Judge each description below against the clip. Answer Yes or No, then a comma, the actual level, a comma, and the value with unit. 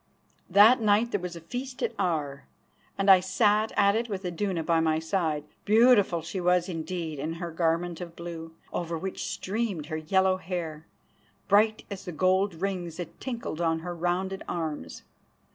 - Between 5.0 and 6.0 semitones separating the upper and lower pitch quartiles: No, average, 3.4 semitones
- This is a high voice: No, medium, 180 Hz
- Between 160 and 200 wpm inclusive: Yes, average, 170 wpm